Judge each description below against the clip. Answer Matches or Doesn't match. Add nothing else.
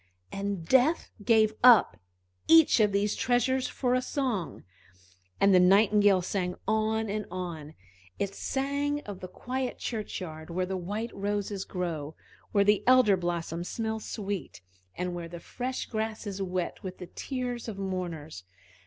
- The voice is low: Doesn't match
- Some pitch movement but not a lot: Matches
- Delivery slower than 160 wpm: Matches